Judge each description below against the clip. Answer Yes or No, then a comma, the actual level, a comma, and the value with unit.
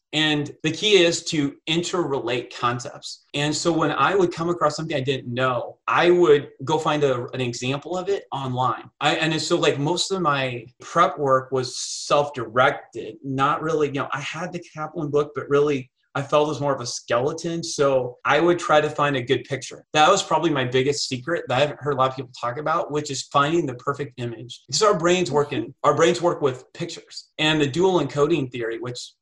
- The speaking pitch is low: No, medium, 145 Hz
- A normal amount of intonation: Yes, average, 3.8 semitones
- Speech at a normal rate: No, fast, 215 wpm